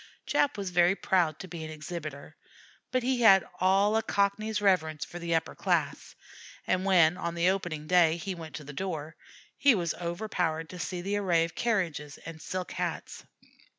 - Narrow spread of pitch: No, average, 3.2 semitones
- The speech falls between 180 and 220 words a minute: Yes, average, 185 wpm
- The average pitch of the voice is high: No, medium, 175 Hz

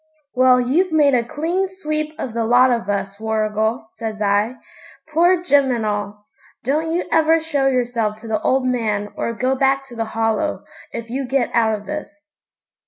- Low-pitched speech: No, very high, 250 Hz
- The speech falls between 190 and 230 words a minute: No, average, 180 wpm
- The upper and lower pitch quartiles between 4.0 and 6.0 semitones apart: Yes, wide, 5.4 semitones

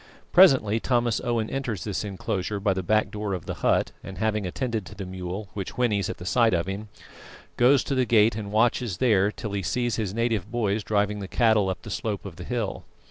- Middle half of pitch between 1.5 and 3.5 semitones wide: Yes, average, 3.1 semitones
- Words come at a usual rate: No, fast, 220 wpm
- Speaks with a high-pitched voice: No, low, 105 Hz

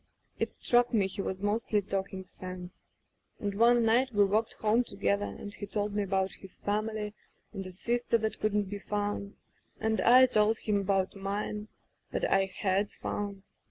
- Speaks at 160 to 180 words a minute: Yes, average, 170 wpm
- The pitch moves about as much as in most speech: No, narrow, 1.9 semitones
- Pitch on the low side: No, high, 205 Hz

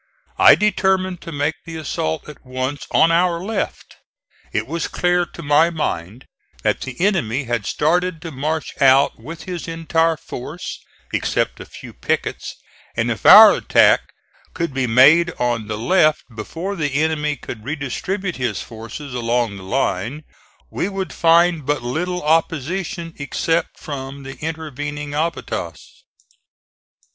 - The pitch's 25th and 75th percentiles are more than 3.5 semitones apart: Yes, average, 4.4 semitones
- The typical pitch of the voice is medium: Yes, medium, 150 Hz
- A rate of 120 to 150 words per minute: Yes, average, 140 wpm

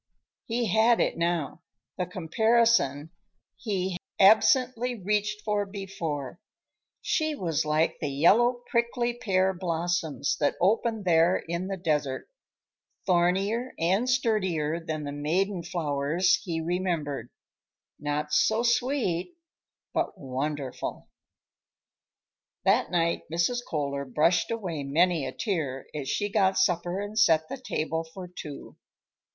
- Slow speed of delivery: Yes, slow, 120 wpm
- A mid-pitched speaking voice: Yes, medium, 175 Hz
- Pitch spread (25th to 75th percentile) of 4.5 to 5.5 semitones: Yes, average, 5.2 semitones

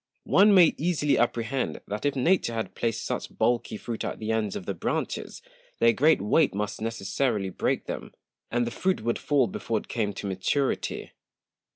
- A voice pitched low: Yes, low, 115 Hz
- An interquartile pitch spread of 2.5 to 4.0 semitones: No, average, 4.7 semitones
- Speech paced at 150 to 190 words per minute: Yes, average, 180 wpm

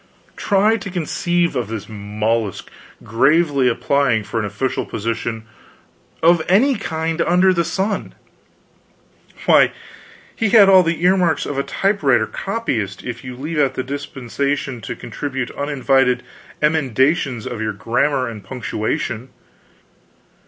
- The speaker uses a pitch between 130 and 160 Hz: Yes, medium, 140 Hz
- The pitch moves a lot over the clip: Yes, wide, 6.5 semitones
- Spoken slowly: Yes, slow, 125 wpm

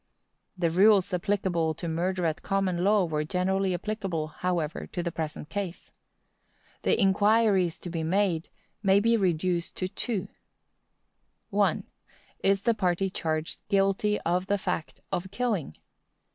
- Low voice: No, medium, 185 Hz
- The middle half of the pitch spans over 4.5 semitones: No, average, 2.8 semitones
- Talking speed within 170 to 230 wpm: No, slow, 135 wpm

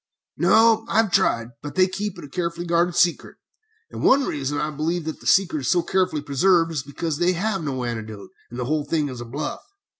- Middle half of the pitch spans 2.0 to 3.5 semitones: No, average, 4.4 semitones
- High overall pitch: No, medium, 165 Hz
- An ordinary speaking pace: No, fast, 220 wpm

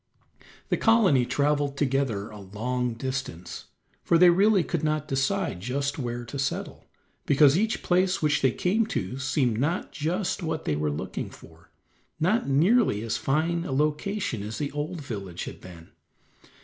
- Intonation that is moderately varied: No, wide, 5.9 semitones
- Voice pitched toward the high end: No, medium, 140 Hz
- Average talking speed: Yes, average, 160 wpm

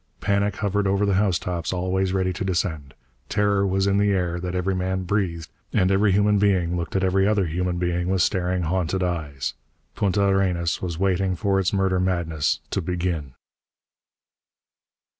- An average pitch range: No, narrow, 1.9 semitones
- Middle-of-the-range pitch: No, very low, 95 Hz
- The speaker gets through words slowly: No, average, 165 wpm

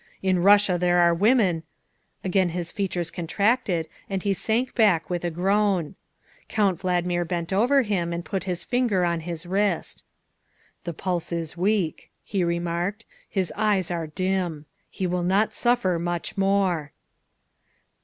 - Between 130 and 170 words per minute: Yes, average, 155 wpm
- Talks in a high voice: No, medium, 180 Hz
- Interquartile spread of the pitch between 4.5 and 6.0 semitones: No, average, 2.7 semitones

